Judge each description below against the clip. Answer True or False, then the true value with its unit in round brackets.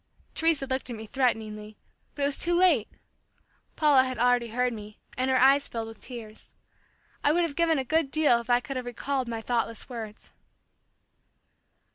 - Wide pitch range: False (3.7 semitones)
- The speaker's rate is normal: True (180 wpm)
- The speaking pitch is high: True (250 Hz)